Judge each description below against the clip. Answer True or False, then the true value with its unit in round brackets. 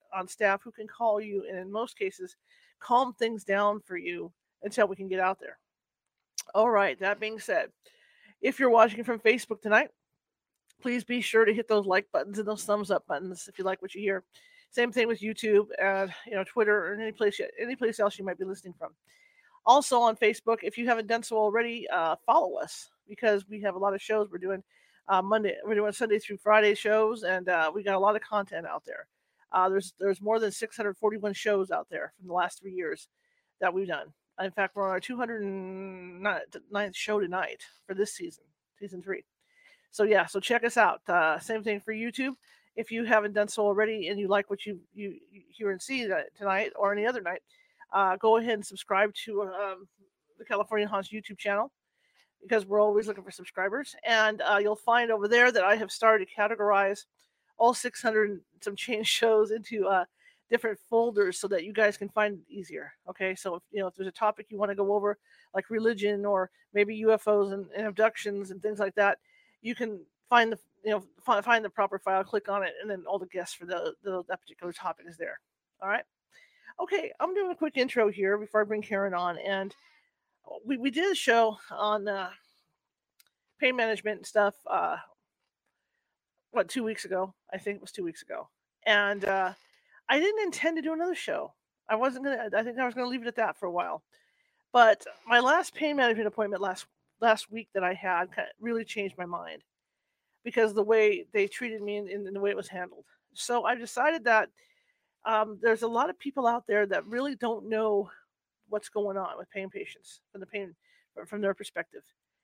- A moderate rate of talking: False (210 wpm)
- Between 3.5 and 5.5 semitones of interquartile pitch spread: False (3.0 semitones)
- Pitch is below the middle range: False (210 Hz)